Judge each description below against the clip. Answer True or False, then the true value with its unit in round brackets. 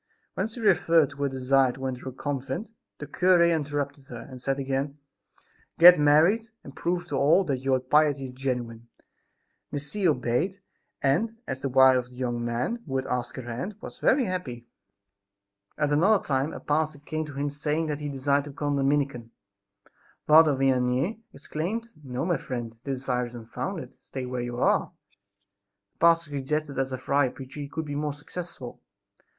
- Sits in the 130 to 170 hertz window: True (140 Hz)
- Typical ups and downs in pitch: True (3.2 semitones)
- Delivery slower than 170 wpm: False (185 wpm)